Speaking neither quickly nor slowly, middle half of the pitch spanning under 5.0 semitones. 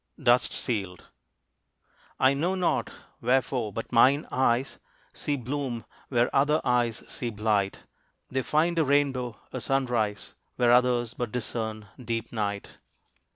No: slow, 125 wpm; average, 3.1 semitones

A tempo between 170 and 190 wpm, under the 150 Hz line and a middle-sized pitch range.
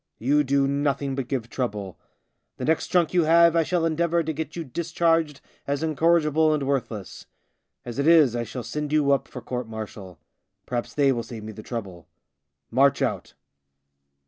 Yes: average, 175 wpm; medium, 140 Hz; average, 5.0 semitones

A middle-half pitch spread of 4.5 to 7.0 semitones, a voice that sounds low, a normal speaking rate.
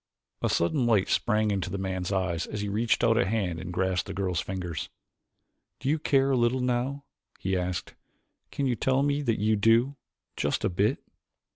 Yes: average, 5.1 semitones; low, 105 Hz; average, 190 wpm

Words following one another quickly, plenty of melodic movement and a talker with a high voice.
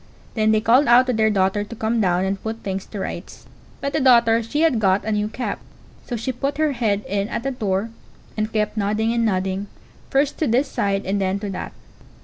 No: fast, 225 wpm; average, 3.3 semitones; high, 220 Hz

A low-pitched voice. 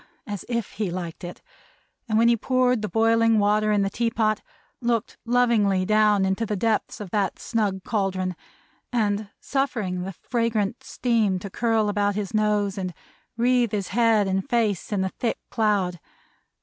No: high, 210 Hz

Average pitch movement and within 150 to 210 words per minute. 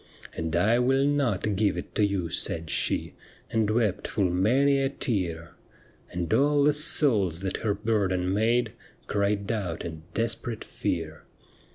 Yes: average, 4.9 semitones; average, 155 wpm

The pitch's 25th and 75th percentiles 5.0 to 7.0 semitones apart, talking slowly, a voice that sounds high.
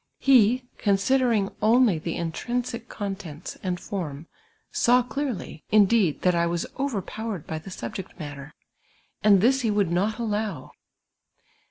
Yes: average, 5.3 semitones; slow, 130 wpm; high, 205 Hz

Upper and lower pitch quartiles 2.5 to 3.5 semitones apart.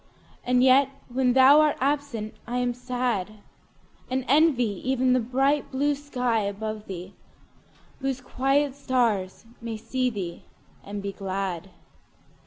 No: average, 4.0 semitones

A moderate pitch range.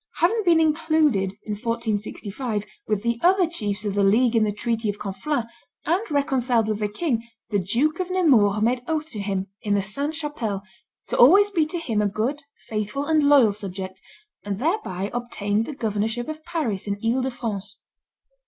No: wide, 6.7 semitones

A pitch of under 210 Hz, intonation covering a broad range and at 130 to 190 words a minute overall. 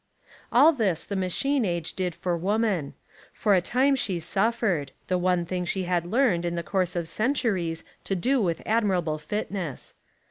No: medium, 185 Hz; average, 4.3 semitones; average, 175 wpm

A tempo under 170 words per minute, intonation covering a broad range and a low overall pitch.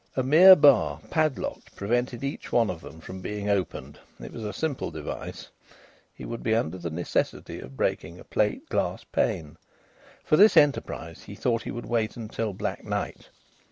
No: average, 175 wpm; wide, 6.9 semitones; low, 110 Hz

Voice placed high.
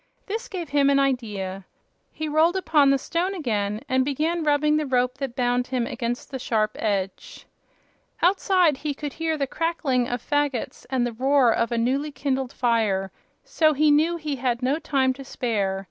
Yes: very high, 270 Hz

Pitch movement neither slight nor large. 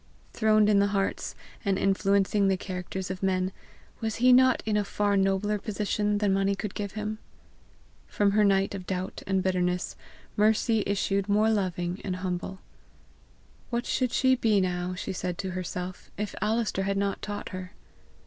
No: narrow, 2.0 semitones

